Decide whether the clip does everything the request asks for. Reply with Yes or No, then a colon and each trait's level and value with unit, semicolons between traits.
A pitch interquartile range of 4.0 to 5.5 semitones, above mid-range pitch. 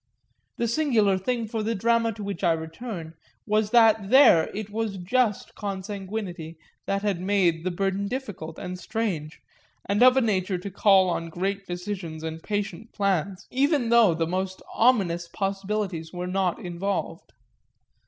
No: average, 3.6 semitones; high, 195 Hz